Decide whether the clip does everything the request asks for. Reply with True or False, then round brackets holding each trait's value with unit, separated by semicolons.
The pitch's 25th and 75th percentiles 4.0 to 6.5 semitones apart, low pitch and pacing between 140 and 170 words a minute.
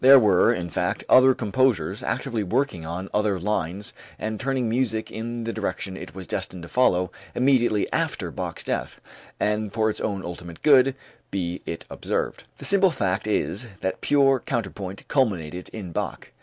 True (5.4 semitones; 105 Hz; 165 wpm)